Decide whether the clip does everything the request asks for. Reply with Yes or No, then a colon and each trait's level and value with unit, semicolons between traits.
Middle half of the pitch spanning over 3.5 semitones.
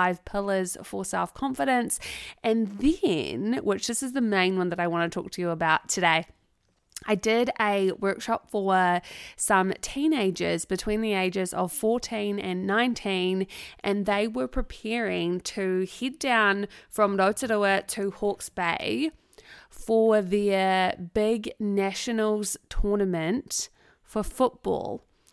No: average, 3.2 semitones